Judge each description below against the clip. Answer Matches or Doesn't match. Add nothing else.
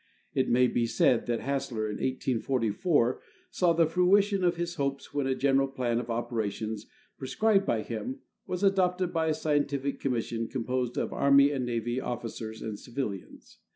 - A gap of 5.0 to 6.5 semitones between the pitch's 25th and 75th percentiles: Matches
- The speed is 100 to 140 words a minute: Doesn't match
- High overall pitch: Doesn't match